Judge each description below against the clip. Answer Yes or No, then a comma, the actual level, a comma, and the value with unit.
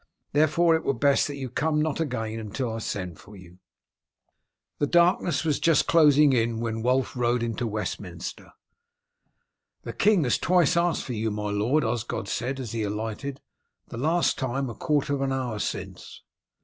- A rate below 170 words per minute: No, average, 175 wpm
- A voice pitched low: Yes, low, 130 Hz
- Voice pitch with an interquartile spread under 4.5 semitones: No, average, 5.1 semitones